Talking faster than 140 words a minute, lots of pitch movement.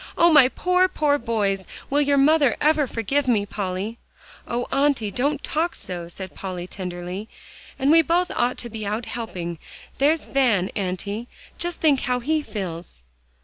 Yes: average, 160 wpm; wide, 6.8 semitones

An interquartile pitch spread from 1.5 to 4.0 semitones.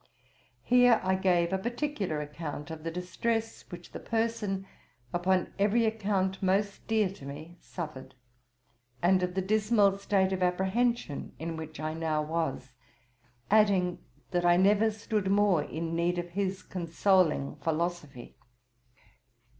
Yes: average, 3.7 semitones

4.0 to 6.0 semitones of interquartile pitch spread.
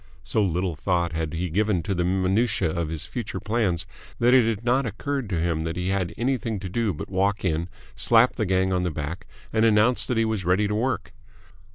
Yes: average, 4.5 semitones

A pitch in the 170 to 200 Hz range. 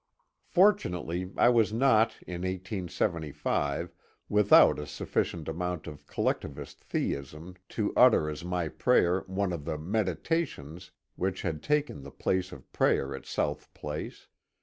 No: very low, 90 Hz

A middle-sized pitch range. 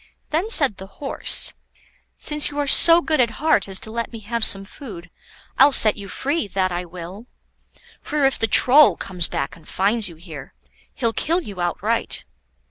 No: wide, 7.3 semitones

